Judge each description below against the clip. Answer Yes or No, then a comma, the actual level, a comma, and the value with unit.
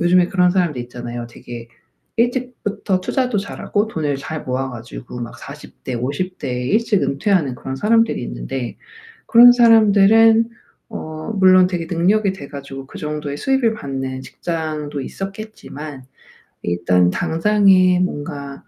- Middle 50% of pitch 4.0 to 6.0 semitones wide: No, wide, 7.4 semitones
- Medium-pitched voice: Yes, medium, 165 Hz